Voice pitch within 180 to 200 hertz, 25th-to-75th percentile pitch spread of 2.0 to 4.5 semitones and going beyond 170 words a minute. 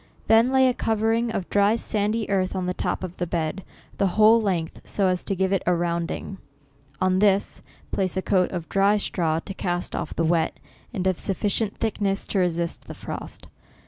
Yes: high, 190 Hz; average, 2.8 semitones; average, 200 wpm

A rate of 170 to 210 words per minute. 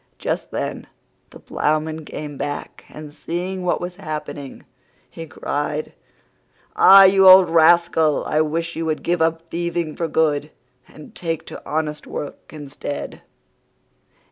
No: slow, 135 wpm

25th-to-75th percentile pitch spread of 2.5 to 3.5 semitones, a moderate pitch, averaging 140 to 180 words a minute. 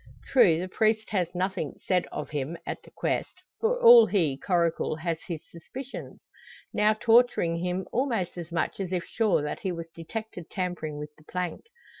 No: average, 4.5 semitones; medium, 180 Hz; average, 175 wpm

